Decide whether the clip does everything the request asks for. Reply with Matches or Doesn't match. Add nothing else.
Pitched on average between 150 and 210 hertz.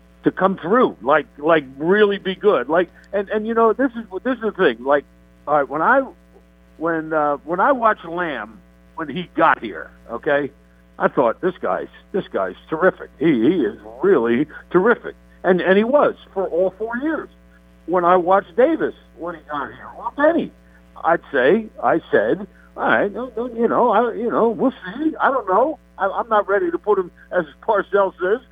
Matches